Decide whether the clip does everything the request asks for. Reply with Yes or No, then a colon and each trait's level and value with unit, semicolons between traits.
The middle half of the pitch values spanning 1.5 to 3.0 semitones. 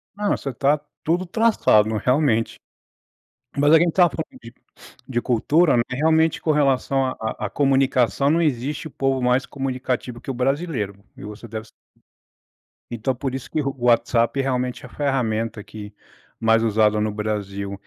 No: average, 4.1 semitones